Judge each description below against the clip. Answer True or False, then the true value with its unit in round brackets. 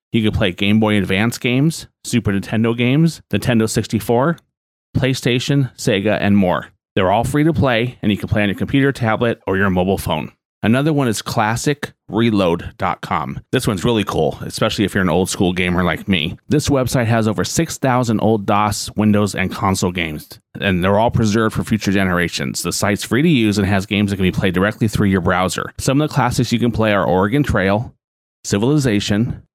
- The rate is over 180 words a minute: True (195 wpm)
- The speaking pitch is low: True (110 Hz)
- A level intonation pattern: False (3.8 semitones)